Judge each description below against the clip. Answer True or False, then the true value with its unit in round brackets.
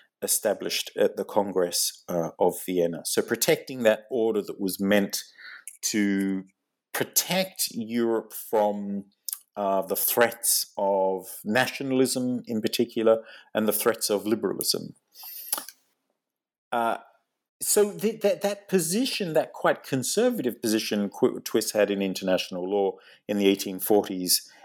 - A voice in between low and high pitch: False (110 Hz)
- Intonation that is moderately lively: False (7.0 semitones)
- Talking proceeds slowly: True (115 wpm)